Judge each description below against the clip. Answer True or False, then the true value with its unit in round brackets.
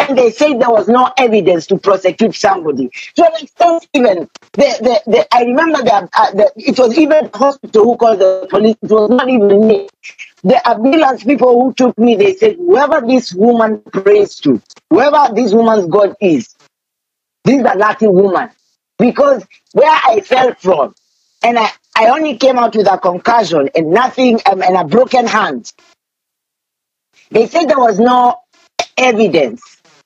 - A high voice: True (240 Hz)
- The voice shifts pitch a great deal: False (4.9 semitones)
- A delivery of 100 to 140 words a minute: False (165 wpm)